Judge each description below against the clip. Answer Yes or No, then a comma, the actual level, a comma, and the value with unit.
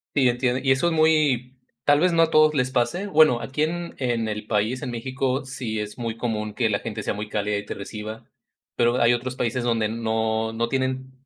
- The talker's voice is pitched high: No, low, 125 Hz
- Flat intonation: No, average, 3.2 semitones